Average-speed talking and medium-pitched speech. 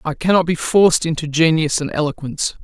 Yes: average, 180 wpm; medium, 160 Hz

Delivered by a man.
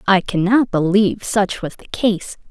No: female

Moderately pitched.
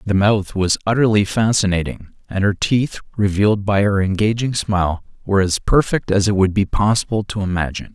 No: low, 100 Hz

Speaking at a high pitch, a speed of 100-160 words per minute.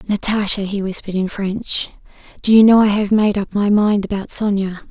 No: high, 205 Hz; average, 195 wpm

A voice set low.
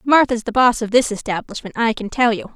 No: high, 230 Hz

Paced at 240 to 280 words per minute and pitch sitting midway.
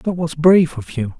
Yes: fast, 250 wpm; medium, 150 Hz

